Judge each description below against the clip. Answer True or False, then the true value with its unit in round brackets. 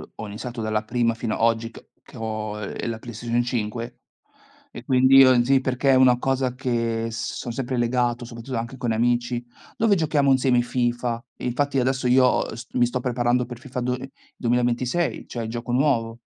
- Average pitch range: False (1.7 semitones)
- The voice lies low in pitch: True (120 Hz)